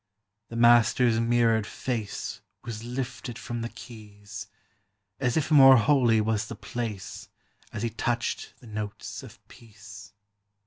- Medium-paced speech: No, slow, 130 wpm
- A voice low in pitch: Yes, low, 115 Hz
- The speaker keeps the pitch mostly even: Yes, narrow, 2.2 semitones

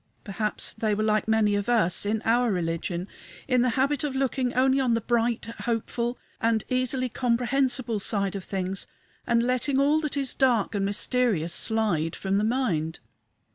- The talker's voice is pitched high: Yes, high, 230 Hz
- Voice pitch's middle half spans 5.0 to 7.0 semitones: No, average, 3.8 semitones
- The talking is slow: No, average, 170 wpm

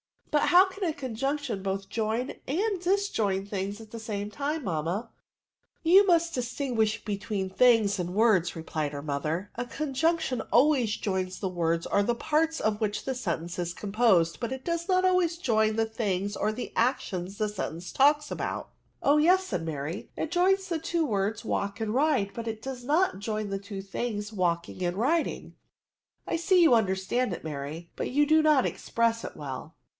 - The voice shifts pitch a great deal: Yes, wide, 7.3 semitones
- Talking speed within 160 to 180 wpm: No, average, 200 wpm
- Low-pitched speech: No, high, 225 Hz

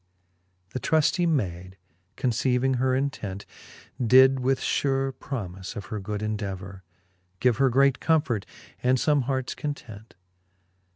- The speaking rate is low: Yes, slow, 125 wpm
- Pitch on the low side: Yes, low, 125 Hz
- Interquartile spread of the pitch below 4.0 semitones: No, average, 4.5 semitones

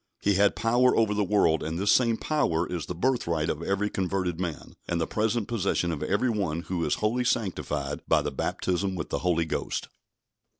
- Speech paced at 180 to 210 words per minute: Yes, average, 200 wpm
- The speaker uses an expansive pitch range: No, average, 4.3 semitones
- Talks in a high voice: No, very low, 95 Hz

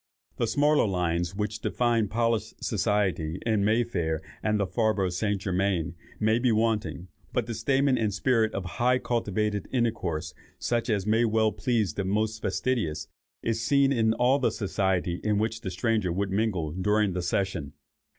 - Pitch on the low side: Yes, low, 105 Hz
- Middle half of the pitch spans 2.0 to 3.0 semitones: No, average, 3.5 semitones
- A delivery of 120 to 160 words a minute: No, average, 170 wpm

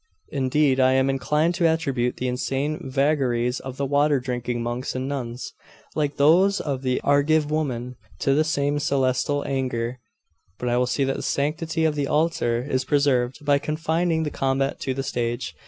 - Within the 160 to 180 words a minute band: Yes, average, 175 wpm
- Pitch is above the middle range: No, low, 135 Hz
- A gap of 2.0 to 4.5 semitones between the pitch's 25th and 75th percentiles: Yes, average, 2.8 semitones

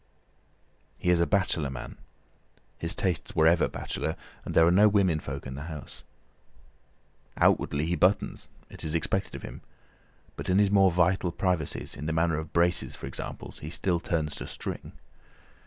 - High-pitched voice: No, very low, 85 Hz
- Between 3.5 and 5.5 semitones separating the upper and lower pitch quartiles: No, average, 2.9 semitones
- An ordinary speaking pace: Yes, average, 160 wpm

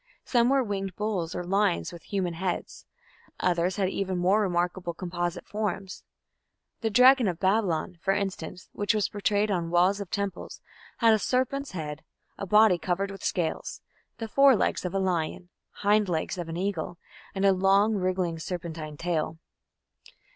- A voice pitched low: No, high, 190 Hz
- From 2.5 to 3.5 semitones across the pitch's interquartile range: Yes, average, 2.8 semitones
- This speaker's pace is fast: No, average, 160 wpm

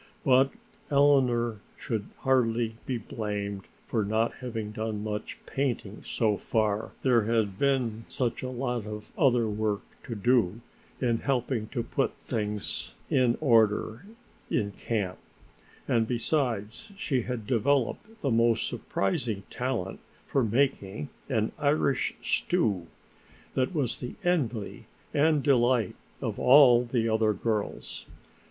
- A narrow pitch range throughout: No, average, 3.3 semitones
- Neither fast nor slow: No, slow, 125 wpm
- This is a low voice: Yes, low, 115 Hz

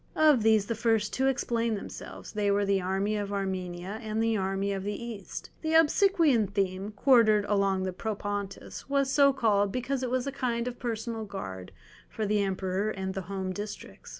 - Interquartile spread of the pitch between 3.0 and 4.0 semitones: Yes, average, 3.4 semitones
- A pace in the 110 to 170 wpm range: No, average, 185 wpm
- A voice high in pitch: Yes, high, 210 Hz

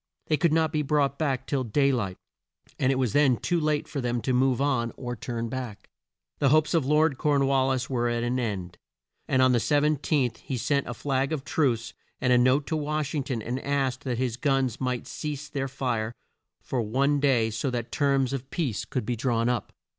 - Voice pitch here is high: No, low, 130 Hz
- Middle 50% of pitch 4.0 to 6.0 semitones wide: No, average, 2.9 semitones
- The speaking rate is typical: No, fast, 220 wpm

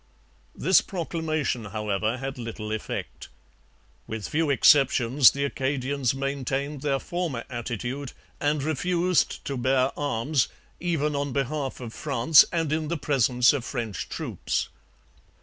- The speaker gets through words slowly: Yes, slow, 125 wpm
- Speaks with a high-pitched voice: No, low, 135 Hz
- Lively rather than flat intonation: No, average, 3.5 semitones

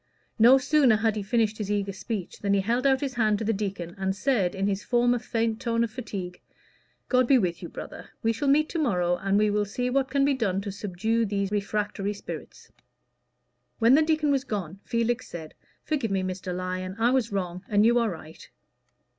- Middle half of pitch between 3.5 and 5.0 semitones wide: Yes, average, 3.9 semitones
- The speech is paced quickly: Yes, fast, 210 wpm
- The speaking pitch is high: Yes, high, 215 Hz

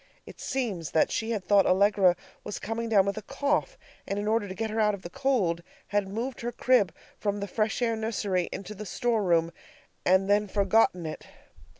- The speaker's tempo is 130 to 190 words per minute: No, fast, 205 wpm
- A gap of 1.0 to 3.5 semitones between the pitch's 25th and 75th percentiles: Yes, average, 2.9 semitones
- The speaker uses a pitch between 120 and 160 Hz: No, high, 205 Hz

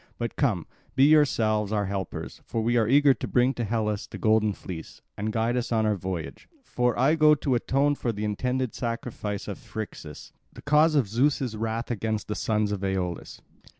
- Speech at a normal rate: Yes, average, 190 wpm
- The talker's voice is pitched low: Yes, low, 115 Hz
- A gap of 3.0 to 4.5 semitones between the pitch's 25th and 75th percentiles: Yes, average, 3.6 semitones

